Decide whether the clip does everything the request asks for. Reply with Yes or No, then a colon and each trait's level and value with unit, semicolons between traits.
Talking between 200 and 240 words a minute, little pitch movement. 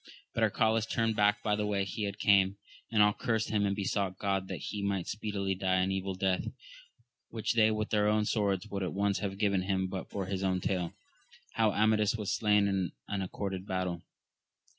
Yes: fast, 205 wpm; narrow, 1.8 semitones